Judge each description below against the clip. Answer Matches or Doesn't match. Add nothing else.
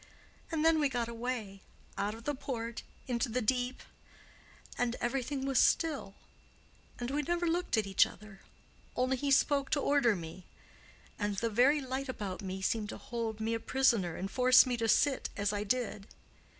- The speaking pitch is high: Matches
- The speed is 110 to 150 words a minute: Doesn't match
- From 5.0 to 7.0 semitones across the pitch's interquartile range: Doesn't match